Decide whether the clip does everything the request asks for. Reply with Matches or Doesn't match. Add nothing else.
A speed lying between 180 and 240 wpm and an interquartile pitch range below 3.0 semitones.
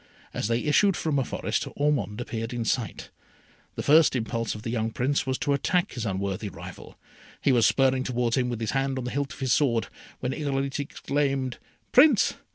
Doesn't match